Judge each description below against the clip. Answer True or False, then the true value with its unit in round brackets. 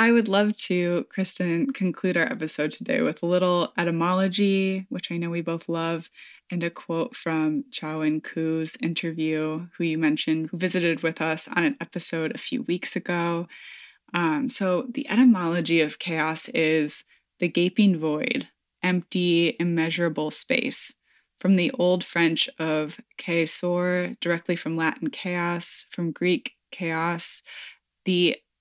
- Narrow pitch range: True (2.1 semitones)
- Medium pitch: True (170 Hz)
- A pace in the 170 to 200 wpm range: False (145 wpm)